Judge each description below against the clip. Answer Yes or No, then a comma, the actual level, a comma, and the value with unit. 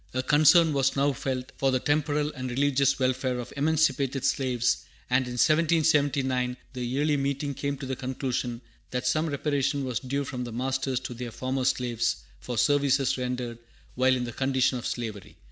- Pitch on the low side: Yes, low, 130 Hz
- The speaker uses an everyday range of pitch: No, narrow, 2.1 semitones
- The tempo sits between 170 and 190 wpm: Yes, average, 180 wpm